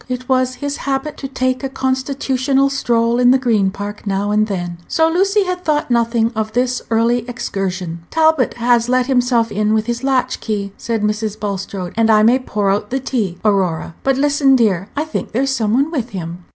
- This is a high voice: Yes, high, 240 Hz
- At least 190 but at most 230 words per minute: Yes, average, 195 wpm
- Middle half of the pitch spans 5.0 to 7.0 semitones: No, average, 4.2 semitones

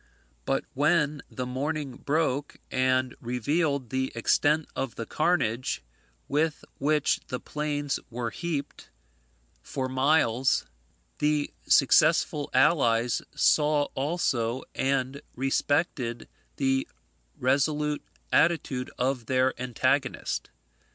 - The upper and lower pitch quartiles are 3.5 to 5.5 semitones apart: No, average, 2.7 semitones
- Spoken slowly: Yes, slow, 95 wpm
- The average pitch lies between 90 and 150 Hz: Yes, low, 135 Hz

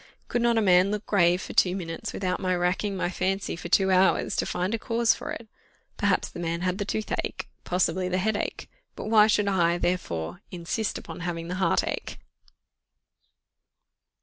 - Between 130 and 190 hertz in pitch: Yes, medium, 185 Hz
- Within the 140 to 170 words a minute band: No, average, 180 wpm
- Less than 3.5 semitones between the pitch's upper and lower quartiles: Yes, average, 2.7 semitones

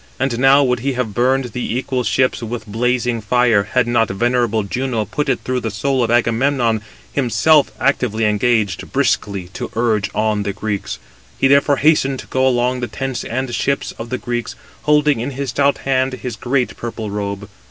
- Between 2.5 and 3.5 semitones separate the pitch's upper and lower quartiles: Yes, average, 3.0 semitones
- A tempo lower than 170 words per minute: No, average, 185 wpm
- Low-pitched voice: Yes, low, 120 Hz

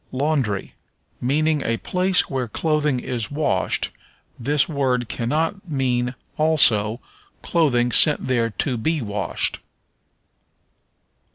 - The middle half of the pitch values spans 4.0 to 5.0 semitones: Yes, average, 4.3 semitones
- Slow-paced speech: Yes, slow, 100 wpm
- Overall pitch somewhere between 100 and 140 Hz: Yes, low, 135 Hz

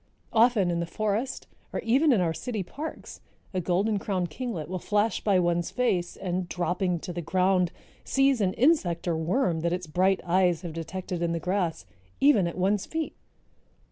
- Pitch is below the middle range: No, medium, 185 Hz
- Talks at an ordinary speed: Yes, average, 180 wpm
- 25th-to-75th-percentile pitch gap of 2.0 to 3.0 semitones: No, average, 3.8 semitones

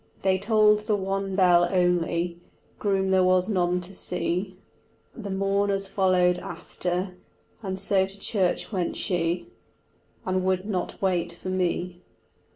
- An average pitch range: No, narrow, 1.6 semitones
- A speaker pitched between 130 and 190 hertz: Yes, medium, 185 Hz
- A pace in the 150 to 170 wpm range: No, slow, 135 wpm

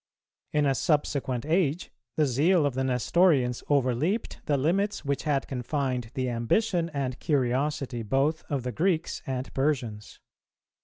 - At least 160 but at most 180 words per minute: No, average, 140 wpm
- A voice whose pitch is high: No, medium, 140 Hz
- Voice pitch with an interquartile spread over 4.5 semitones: No, average, 3.6 semitones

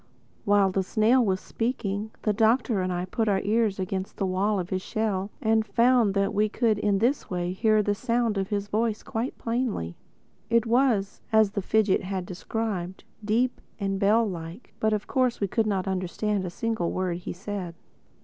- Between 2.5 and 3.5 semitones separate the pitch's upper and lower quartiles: Yes, average, 2.9 semitones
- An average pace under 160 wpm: No, average, 190 wpm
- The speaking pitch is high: Yes, high, 205 Hz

